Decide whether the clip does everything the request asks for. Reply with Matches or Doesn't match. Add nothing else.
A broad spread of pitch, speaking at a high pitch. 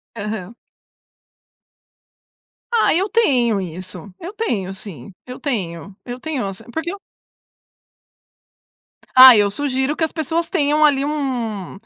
Matches